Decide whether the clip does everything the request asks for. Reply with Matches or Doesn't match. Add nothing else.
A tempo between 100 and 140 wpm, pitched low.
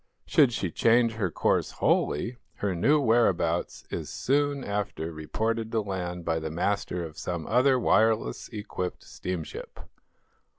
Matches